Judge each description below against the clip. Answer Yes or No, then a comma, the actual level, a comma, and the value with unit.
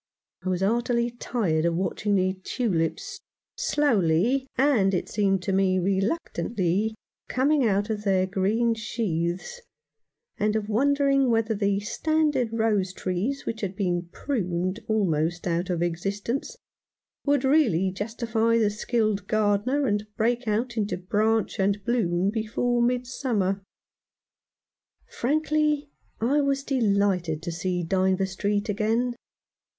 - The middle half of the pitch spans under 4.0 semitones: No, average, 4.3 semitones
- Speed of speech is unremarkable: No, slow, 125 wpm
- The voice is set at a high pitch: Yes, high, 210 Hz